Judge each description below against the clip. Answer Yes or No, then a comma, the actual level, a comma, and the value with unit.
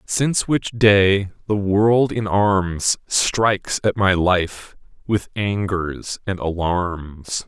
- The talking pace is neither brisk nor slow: No, slow, 120 wpm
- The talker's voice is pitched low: Yes, low, 100 Hz